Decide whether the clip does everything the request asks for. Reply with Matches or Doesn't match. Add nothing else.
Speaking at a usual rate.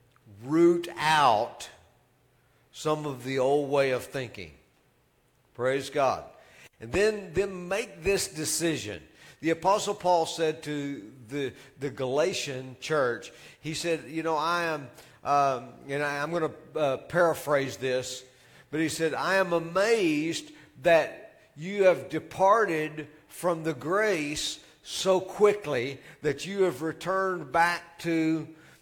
Doesn't match